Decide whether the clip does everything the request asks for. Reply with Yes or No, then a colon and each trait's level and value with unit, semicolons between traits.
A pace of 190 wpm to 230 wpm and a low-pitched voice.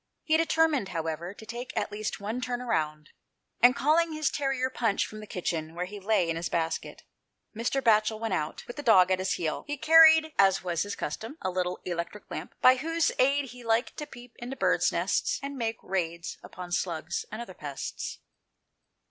No: average, 195 wpm; high, 220 Hz